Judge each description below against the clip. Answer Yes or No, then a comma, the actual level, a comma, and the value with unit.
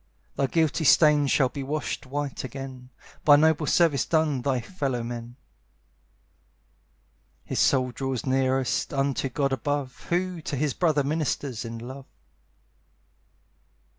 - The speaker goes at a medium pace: No, slow, 125 wpm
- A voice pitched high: No, medium, 140 Hz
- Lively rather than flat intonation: No, narrow, 2.6 semitones